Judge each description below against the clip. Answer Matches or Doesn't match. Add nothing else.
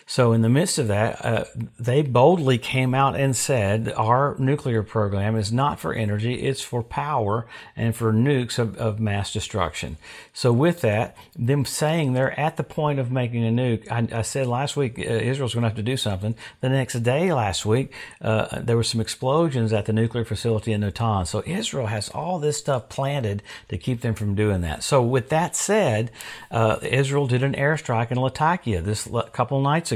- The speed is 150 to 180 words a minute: Doesn't match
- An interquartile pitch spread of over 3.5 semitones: Matches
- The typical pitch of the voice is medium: Doesn't match